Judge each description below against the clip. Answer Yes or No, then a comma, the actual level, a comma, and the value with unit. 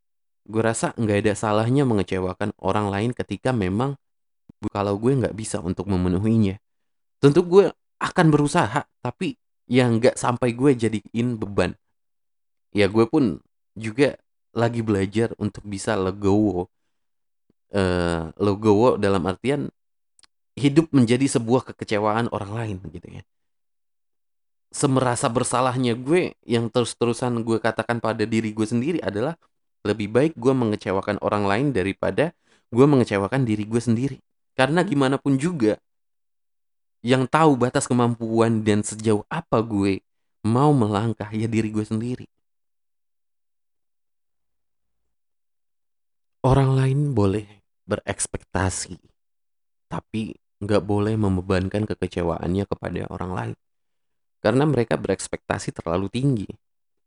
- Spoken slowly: No, average, 115 wpm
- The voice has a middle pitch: No, low, 110 Hz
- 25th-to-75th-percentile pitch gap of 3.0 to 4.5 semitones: Yes, average, 3.9 semitones